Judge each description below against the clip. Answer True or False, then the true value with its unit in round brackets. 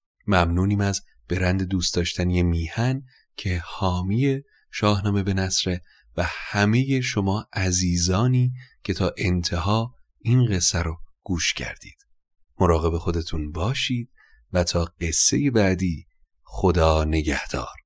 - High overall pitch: False (95 Hz)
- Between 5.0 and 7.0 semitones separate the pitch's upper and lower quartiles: False (3.8 semitones)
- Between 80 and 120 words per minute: True (110 wpm)